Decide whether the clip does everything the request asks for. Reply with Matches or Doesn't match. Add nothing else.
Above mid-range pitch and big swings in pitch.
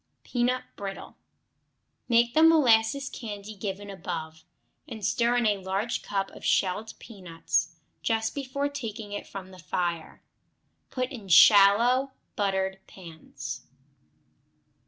Doesn't match